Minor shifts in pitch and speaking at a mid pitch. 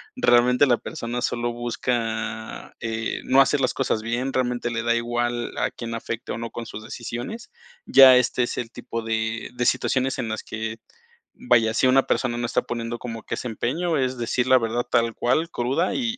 No: narrow, 1.9 semitones; low, 120 Hz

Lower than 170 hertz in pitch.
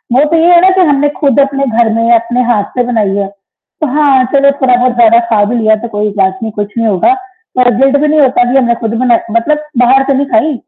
No: very high, 250 Hz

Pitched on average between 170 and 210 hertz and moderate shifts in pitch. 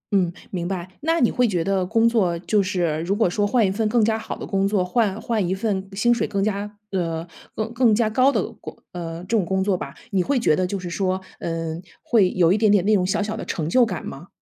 Yes: high, 195 Hz; average, 3.4 semitones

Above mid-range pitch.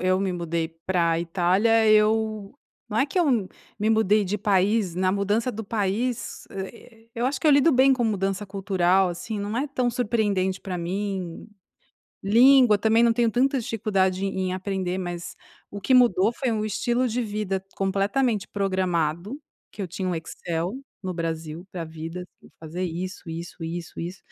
Yes: high, 195 Hz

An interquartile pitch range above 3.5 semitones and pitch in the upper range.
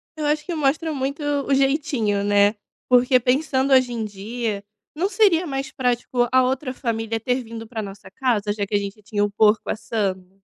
Yes: average, 4.5 semitones; high, 245 Hz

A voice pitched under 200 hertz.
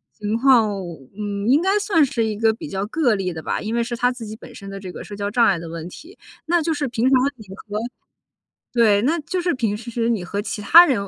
No: high, 230 Hz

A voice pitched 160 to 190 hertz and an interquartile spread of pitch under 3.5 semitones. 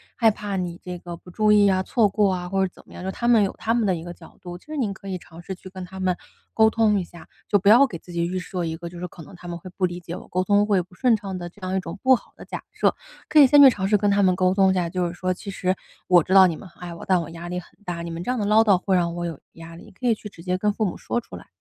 Yes: medium, 185 Hz; average, 2.9 semitones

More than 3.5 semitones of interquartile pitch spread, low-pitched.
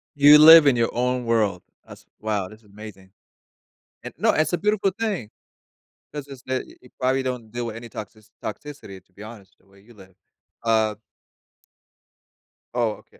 Yes: average, 4.6 semitones; low, 115 Hz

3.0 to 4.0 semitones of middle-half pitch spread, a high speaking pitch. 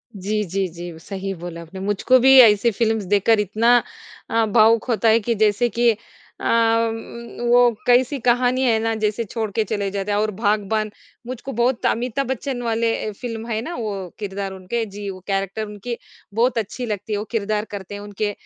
No: narrow, 2.6 semitones; high, 220 Hz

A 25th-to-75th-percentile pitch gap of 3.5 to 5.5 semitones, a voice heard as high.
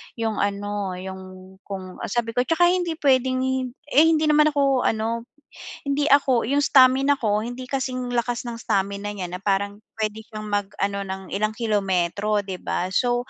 Yes: average, 4.5 semitones; high, 220 Hz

